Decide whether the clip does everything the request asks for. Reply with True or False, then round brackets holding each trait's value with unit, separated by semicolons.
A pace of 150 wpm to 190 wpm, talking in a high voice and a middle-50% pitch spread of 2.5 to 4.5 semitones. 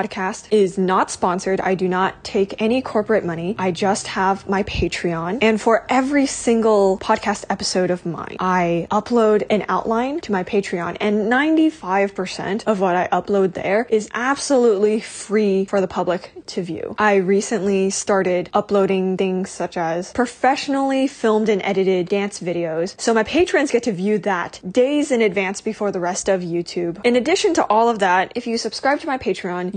True (175 wpm; 200 Hz; 3.3 semitones)